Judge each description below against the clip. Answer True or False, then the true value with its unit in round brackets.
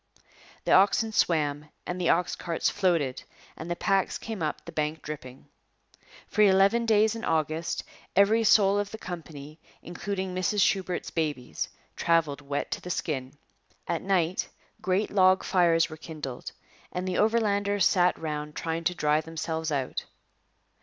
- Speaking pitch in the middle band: True (175 Hz)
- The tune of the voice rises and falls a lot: False (4.0 semitones)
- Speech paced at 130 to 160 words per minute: True (150 wpm)